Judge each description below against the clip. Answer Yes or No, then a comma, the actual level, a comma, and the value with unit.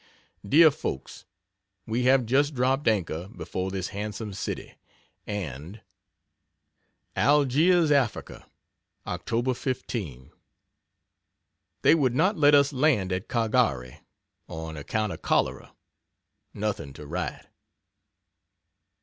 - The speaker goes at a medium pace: No, slow, 100 wpm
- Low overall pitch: Yes, low, 110 Hz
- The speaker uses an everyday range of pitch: No, wide, 6.7 semitones